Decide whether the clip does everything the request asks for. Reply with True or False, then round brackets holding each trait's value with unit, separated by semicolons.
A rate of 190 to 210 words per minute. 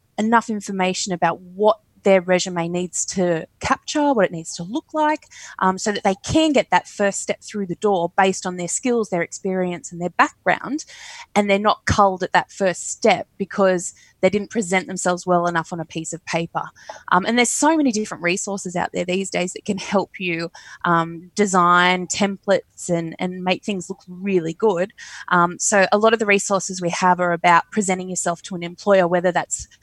True (200 wpm)